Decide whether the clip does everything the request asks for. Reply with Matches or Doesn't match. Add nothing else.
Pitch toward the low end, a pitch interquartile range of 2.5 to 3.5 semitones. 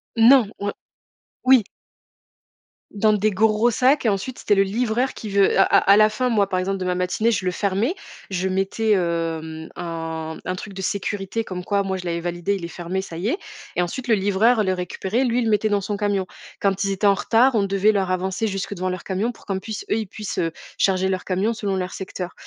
Doesn't match